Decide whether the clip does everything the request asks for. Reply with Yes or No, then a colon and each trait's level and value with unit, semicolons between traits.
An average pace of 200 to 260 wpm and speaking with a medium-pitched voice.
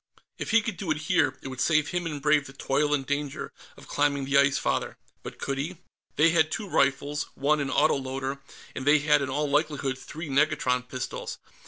Yes: fast, 205 wpm; medium, 145 Hz